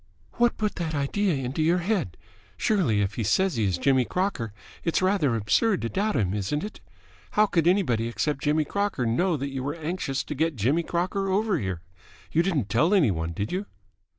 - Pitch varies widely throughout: Yes, wide, 8.3 semitones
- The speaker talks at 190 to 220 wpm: Yes, average, 200 wpm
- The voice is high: No, medium, 155 Hz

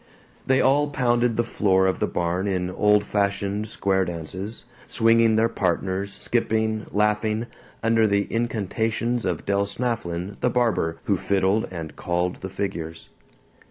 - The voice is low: Yes, low, 105 Hz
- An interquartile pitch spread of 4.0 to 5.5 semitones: No, average, 3.4 semitones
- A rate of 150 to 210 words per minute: No, average, 140 wpm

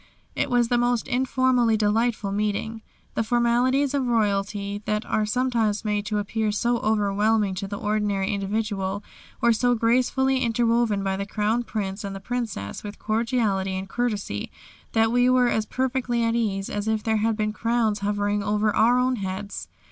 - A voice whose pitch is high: Yes, high, 220 Hz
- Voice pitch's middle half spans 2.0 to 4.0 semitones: Yes, average, 2.8 semitones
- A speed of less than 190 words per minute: Yes, average, 170 wpm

